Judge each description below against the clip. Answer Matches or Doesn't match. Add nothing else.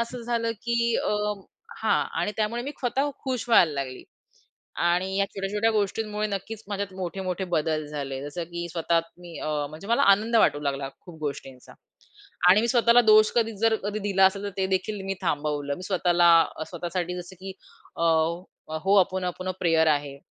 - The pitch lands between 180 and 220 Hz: Matches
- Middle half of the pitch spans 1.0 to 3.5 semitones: Doesn't match